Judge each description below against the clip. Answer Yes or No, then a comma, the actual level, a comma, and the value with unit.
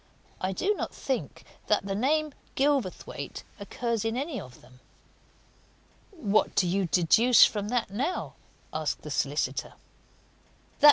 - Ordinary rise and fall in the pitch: No, wide, 5.9 semitones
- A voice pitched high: Yes, high, 225 Hz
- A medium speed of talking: No, slow, 120 wpm